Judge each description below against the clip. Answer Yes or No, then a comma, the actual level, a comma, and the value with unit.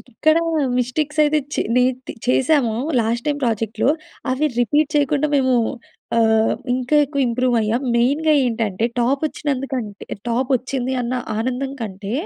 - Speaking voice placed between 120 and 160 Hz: No, very high, 255 Hz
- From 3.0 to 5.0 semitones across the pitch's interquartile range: Yes, average, 3.6 semitones